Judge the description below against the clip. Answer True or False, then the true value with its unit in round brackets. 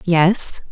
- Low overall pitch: False (175 Hz)